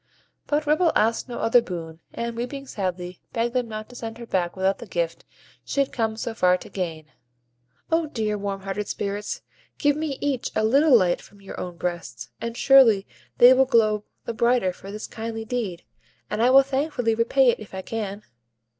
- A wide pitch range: No, average, 4.3 semitones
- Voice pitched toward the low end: No, high, 225 Hz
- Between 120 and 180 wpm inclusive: No, average, 195 wpm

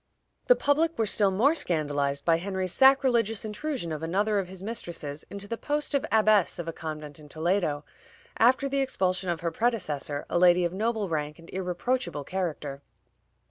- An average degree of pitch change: No, wide, 6.0 semitones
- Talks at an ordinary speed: Yes, average, 175 wpm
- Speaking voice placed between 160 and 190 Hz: Yes, medium, 185 Hz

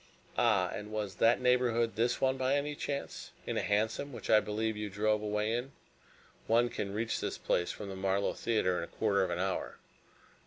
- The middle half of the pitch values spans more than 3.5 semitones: No, average, 3.0 semitones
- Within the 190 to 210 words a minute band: Yes, average, 200 wpm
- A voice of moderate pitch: No, low, 110 Hz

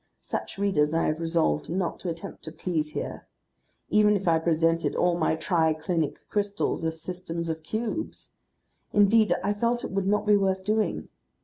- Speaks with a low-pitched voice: No, medium, 175 Hz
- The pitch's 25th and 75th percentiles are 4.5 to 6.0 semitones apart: No, average, 4.0 semitones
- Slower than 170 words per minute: No, average, 175 wpm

